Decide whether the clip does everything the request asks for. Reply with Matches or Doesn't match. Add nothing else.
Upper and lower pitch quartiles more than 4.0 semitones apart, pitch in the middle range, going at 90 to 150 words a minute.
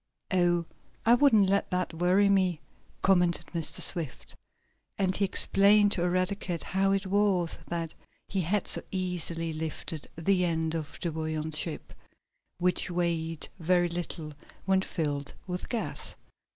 Doesn't match